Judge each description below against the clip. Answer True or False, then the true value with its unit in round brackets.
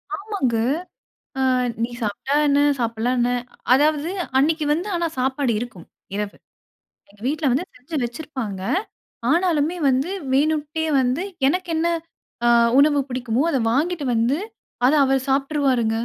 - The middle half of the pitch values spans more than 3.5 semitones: True (4.2 semitones)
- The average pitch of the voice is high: True (275 Hz)